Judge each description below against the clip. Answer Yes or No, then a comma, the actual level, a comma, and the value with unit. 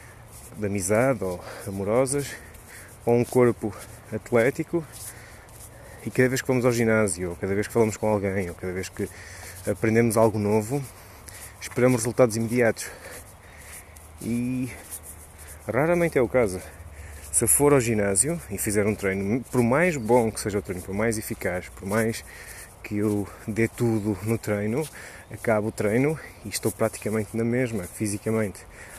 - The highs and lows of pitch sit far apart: No, average, 3.3 semitones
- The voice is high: No, low, 110 Hz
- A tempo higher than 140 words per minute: Yes, average, 150 wpm